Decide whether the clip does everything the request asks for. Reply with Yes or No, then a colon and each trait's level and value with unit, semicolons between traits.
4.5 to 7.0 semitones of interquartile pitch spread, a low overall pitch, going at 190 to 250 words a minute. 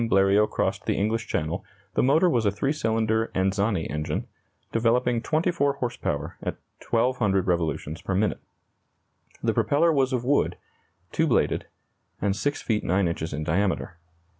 No: average, 5.2 semitones; low, 110 Hz; average, 150 wpm